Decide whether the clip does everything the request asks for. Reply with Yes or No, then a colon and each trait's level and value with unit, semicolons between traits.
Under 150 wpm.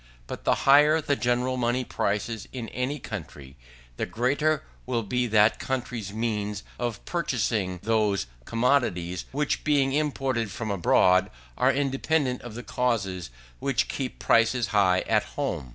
Yes: average, 140 wpm